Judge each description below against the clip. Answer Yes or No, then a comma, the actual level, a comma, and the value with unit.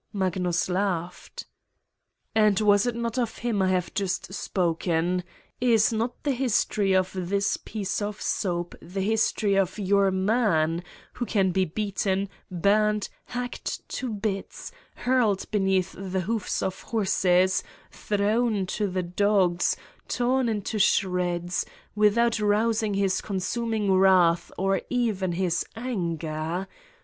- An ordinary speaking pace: No, slow, 125 wpm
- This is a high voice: Yes, high, 195 Hz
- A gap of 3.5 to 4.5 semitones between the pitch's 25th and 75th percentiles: No, average, 2.8 semitones